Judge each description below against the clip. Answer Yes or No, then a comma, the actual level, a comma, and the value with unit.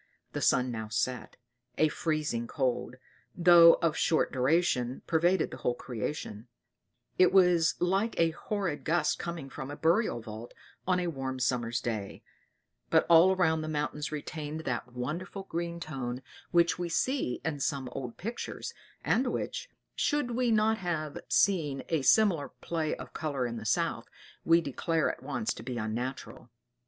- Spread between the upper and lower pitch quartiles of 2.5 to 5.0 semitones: No, wide, 5.5 semitones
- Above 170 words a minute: No, average, 155 wpm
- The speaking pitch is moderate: Yes, medium, 155 Hz